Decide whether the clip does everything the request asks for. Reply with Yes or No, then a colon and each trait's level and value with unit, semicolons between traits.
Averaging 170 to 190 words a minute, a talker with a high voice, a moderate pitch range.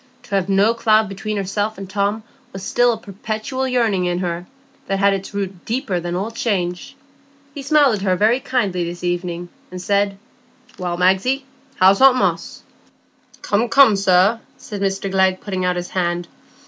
Yes: average, 175 wpm; high, 195 Hz; average, 3.3 semitones